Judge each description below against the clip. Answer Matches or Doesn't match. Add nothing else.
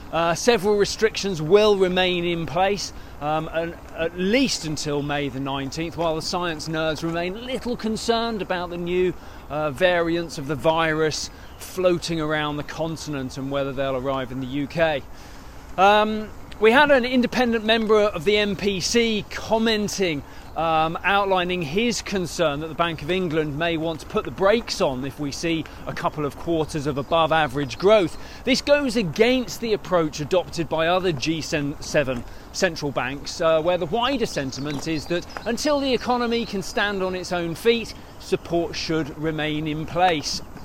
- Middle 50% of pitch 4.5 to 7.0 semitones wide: Matches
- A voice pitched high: Doesn't match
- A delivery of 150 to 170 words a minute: Matches